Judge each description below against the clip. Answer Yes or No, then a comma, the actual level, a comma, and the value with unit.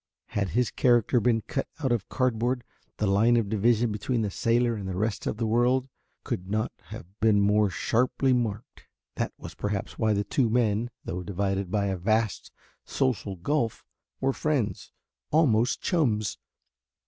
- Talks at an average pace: Yes, average, 160 wpm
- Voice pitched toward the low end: Yes, low, 110 Hz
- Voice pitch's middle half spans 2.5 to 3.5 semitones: Yes, average, 3.2 semitones